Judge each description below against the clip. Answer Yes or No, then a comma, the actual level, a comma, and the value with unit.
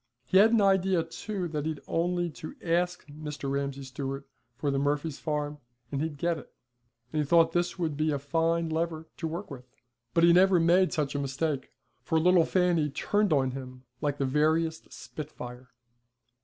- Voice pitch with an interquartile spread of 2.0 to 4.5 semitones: Yes, average, 3.2 semitones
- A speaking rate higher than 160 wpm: Yes, average, 185 wpm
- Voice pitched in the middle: Yes, medium, 155 Hz